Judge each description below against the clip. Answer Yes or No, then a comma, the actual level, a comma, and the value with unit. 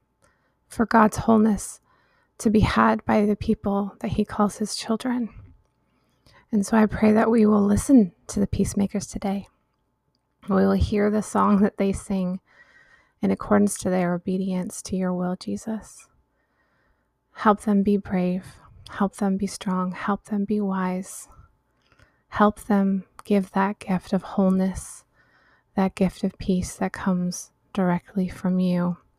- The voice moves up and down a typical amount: No, narrow, 2.3 semitones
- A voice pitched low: No, high, 195 Hz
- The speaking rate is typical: Yes, average, 145 wpm